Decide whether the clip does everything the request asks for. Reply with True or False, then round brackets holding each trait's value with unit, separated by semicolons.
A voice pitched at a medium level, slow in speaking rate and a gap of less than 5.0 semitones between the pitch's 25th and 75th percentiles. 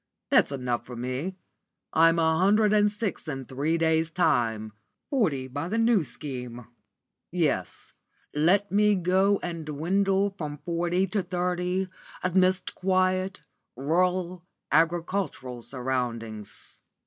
False (170 Hz; 120 wpm; 5.4 semitones)